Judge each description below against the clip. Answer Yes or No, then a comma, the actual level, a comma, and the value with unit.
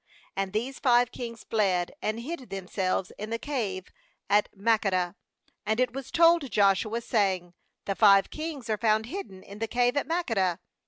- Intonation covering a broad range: No, average, 4.1 semitones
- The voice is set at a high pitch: Yes, high, 220 Hz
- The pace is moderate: Yes, average, 165 wpm